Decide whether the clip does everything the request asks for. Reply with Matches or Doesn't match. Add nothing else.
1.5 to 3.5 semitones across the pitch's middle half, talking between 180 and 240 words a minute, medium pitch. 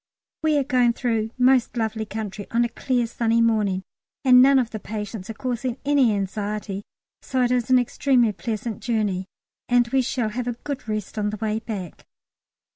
Doesn't match